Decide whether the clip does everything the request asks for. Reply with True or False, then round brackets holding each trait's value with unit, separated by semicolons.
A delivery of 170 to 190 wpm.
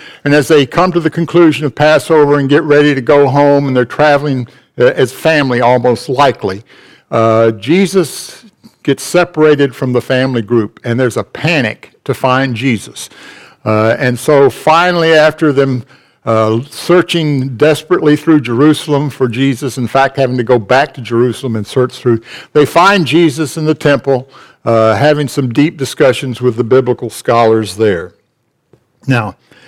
False (160 wpm)